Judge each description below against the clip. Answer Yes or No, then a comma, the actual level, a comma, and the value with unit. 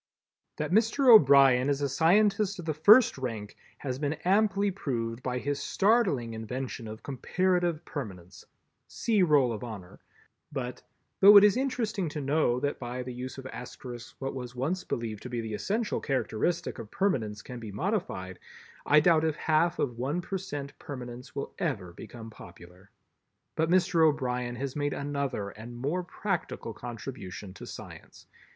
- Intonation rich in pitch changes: Yes, wide, 6.5 semitones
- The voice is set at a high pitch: No, low, 135 Hz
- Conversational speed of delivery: Yes, average, 160 wpm